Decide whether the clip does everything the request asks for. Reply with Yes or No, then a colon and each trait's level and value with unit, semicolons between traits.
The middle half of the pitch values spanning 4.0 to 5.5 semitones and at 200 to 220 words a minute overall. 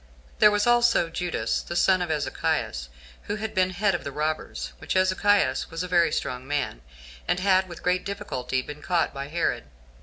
Yes: average, 4.5 semitones; fast, 205 wpm